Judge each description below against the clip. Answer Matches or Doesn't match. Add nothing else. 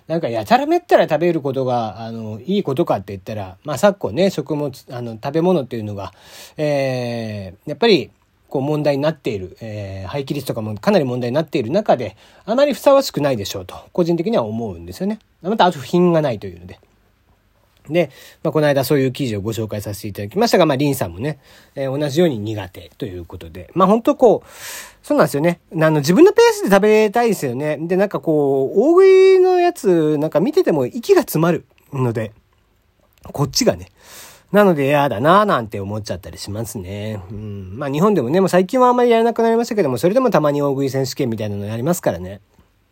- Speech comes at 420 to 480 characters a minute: Matches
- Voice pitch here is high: Doesn't match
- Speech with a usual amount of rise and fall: Doesn't match